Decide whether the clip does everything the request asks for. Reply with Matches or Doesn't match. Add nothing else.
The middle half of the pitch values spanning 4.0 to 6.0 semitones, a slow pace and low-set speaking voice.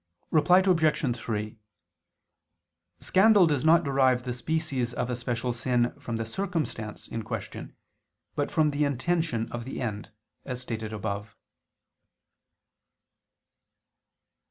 Matches